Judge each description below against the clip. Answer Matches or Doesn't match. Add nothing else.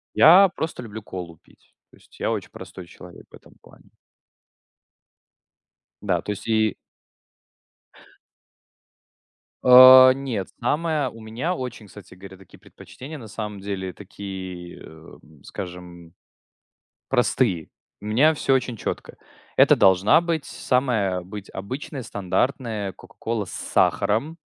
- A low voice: Matches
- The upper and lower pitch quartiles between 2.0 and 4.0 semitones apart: Doesn't match